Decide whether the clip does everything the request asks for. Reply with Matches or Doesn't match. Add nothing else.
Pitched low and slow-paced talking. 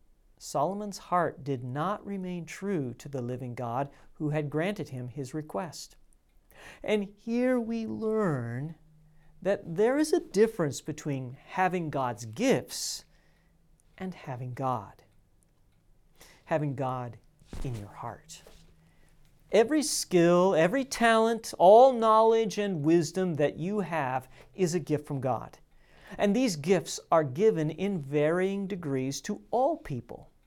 Doesn't match